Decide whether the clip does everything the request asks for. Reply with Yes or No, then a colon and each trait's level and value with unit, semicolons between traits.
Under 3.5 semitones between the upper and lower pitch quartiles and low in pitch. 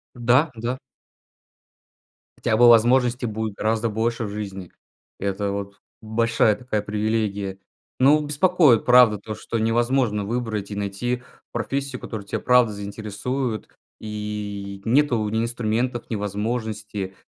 Yes: average, 2.8 semitones; low, 110 Hz